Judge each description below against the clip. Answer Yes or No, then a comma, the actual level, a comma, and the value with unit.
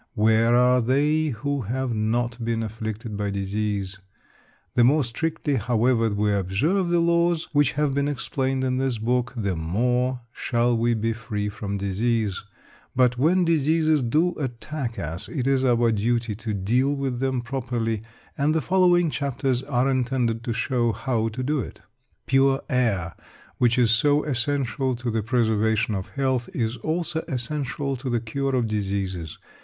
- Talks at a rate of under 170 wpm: Yes, average, 160 wpm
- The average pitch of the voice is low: Yes, low, 120 Hz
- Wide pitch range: No, average, 3.6 semitones